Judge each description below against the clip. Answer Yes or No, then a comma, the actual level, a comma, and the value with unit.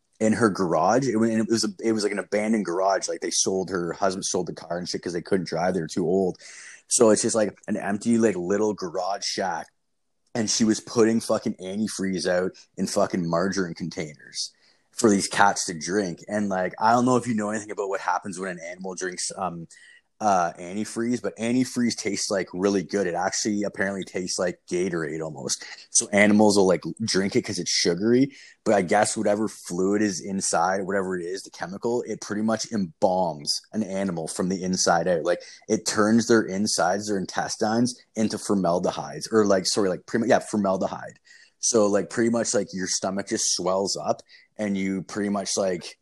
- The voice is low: Yes, low, 105 Hz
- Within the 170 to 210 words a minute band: Yes, average, 200 wpm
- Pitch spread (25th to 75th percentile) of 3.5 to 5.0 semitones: No, average, 2.7 semitones